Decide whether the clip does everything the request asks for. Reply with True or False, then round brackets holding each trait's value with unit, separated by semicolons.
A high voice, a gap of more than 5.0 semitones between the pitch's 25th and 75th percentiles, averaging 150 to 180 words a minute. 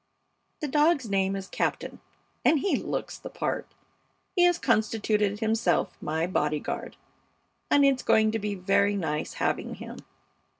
False (210 Hz; 5.5 semitones; 140 wpm)